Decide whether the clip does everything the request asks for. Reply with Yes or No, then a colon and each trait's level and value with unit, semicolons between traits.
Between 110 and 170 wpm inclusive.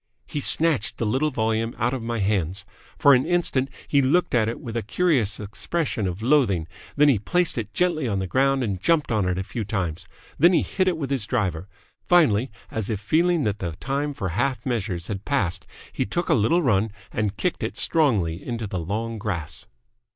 No: fast, 205 wpm